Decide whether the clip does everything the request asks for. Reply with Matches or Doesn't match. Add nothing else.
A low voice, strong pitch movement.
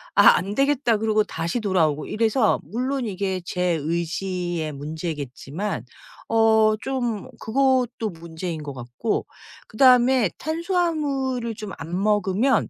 Doesn't match